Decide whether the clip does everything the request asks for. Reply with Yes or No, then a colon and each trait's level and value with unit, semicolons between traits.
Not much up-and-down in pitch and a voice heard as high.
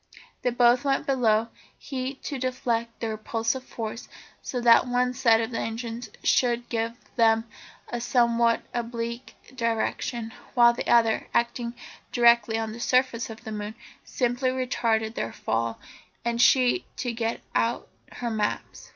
Yes: narrow, 1.5 semitones; high, 235 Hz